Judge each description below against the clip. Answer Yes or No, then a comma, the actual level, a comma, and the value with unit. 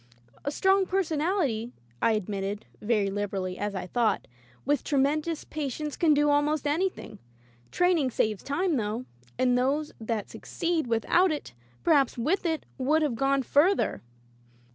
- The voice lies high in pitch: Yes, very high, 280 Hz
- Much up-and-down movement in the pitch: Yes, wide, 5.7 semitones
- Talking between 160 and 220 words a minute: No, average, 140 wpm